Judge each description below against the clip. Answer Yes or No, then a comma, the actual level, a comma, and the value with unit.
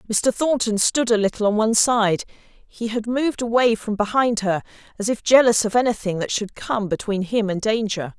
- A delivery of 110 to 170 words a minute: No, average, 200 wpm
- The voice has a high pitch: Yes, high, 220 Hz